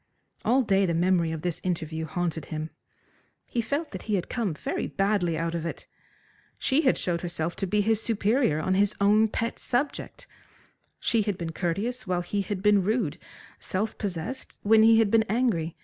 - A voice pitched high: Yes, high, 195 Hz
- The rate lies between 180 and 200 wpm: Yes, average, 185 wpm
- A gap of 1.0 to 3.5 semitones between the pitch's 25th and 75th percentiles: No, average, 4.6 semitones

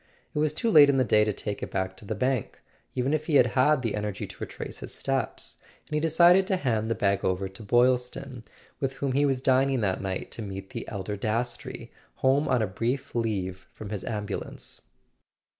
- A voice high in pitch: No, low, 120 Hz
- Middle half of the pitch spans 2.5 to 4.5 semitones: No, average, 4.9 semitones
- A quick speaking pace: Yes, fast, 210 wpm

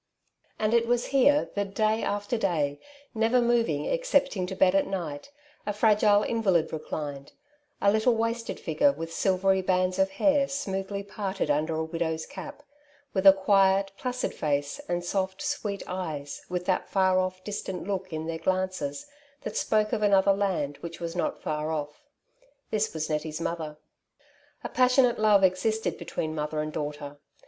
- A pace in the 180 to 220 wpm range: No, average, 165 wpm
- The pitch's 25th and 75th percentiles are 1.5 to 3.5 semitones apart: No, average, 5.0 semitones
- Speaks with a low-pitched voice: No, high, 190 Hz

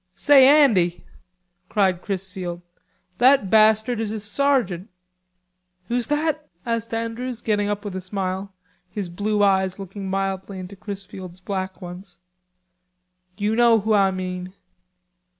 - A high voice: Yes, high, 200 Hz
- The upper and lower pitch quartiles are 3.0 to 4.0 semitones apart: Yes, average, 3.3 semitones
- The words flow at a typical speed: No, slow, 125 wpm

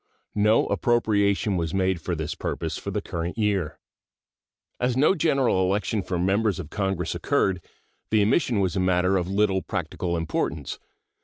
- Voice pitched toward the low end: Yes, very low, 95 Hz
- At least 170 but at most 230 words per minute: No, average, 155 wpm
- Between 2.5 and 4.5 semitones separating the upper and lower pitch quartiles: Yes, average, 3.0 semitones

